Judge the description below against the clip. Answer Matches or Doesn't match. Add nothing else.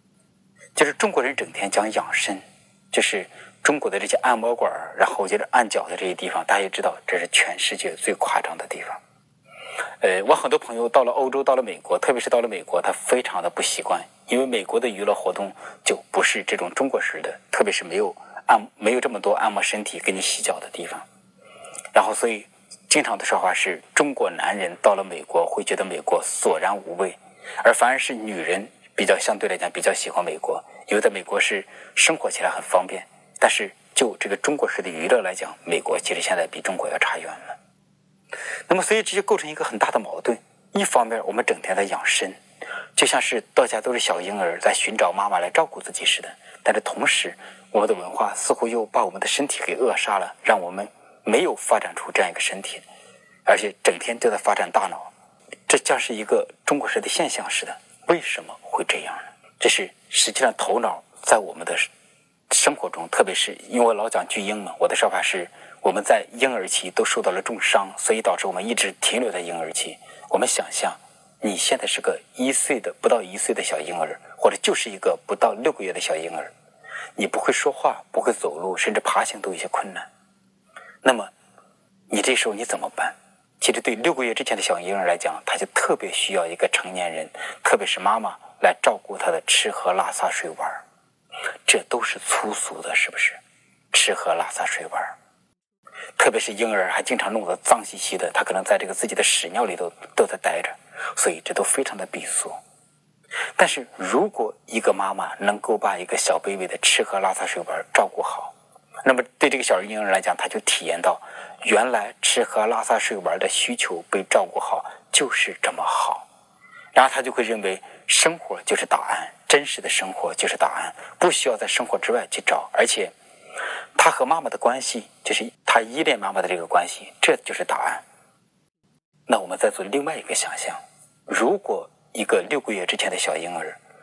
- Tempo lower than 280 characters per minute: Doesn't match